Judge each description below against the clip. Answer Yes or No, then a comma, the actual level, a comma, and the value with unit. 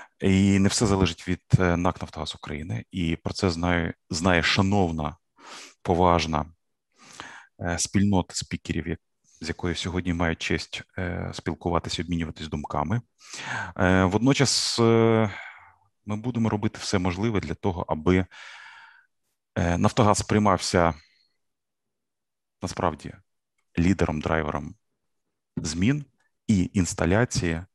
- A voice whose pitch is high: No, very low, 90 Hz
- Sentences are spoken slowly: Yes, slow, 90 wpm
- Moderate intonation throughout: Yes, average, 3.7 semitones